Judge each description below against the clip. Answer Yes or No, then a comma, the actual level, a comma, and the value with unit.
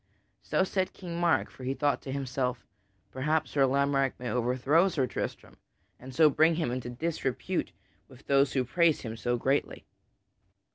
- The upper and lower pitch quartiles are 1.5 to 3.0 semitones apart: No, average, 3.9 semitones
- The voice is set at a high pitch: No, low, 135 Hz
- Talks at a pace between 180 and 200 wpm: No, average, 160 wpm